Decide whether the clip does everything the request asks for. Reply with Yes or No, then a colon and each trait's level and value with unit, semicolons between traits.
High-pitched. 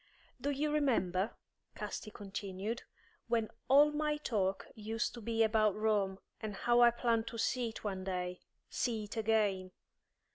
Yes: high, 220 Hz